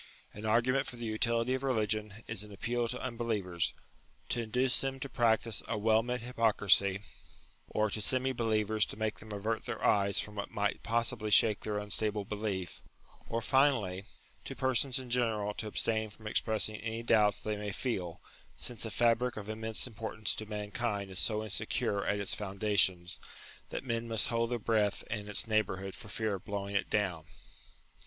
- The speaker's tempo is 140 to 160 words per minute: No, average, 180 wpm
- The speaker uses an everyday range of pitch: No, narrow, 2.2 semitones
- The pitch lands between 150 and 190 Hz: No, low, 110 Hz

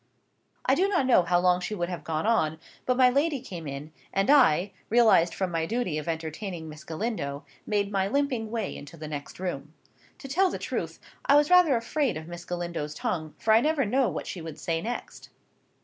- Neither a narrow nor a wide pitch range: No, wide, 7.3 semitones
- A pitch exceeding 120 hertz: Yes, high, 190 Hz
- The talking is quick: Yes, fast, 210 wpm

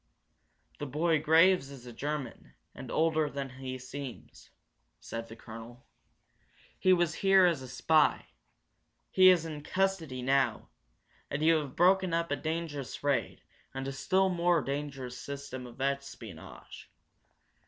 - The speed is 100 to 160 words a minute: Yes, average, 140 wpm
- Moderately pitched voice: Yes, medium, 145 Hz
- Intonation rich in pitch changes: No, average, 4.2 semitones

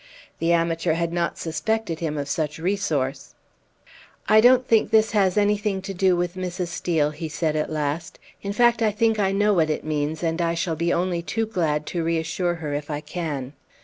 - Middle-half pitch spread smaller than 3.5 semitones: No, average, 4.1 semitones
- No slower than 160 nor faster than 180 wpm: No, average, 200 wpm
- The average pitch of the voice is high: No, medium, 170 Hz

